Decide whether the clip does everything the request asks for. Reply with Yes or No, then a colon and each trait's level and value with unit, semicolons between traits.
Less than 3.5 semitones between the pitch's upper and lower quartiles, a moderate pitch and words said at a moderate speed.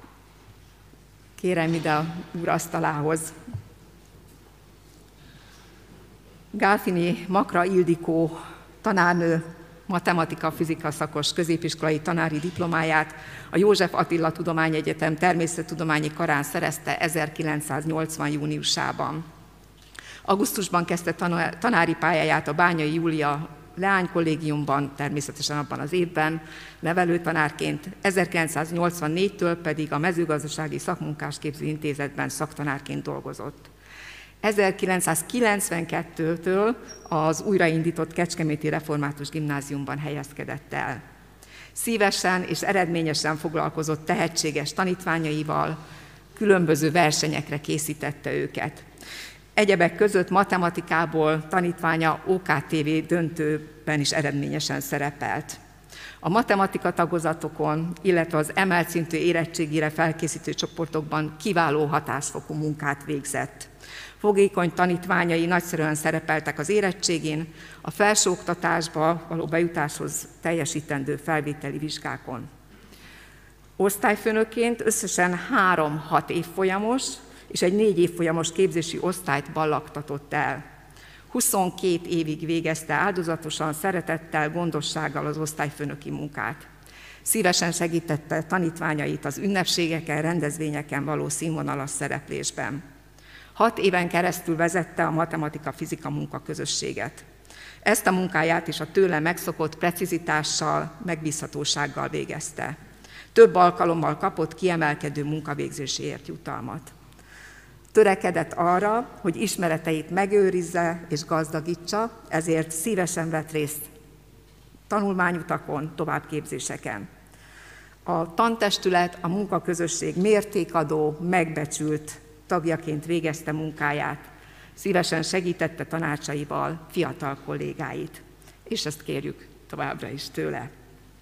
No: narrow, 2.6 semitones; medium, 160 Hz; slow, 85 wpm